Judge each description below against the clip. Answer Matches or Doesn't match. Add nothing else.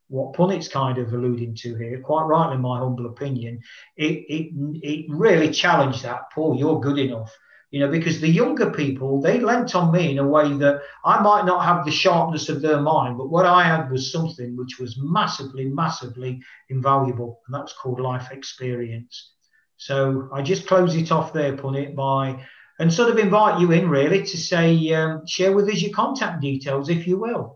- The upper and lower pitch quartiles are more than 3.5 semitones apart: Matches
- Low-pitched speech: Doesn't match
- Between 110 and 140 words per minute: Doesn't match